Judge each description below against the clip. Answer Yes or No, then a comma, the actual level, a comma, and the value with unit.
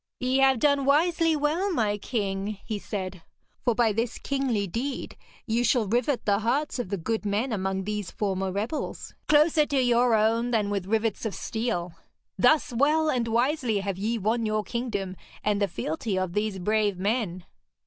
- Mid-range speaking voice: No, high, 225 Hz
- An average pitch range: Yes, average, 4.1 semitones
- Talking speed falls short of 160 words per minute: No, average, 175 wpm